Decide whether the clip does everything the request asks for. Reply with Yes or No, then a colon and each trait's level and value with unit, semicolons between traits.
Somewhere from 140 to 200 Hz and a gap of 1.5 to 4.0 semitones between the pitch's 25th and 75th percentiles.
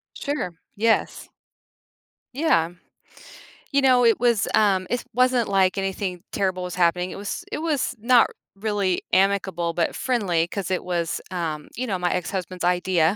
No: high, 190 Hz; average, 4.4 semitones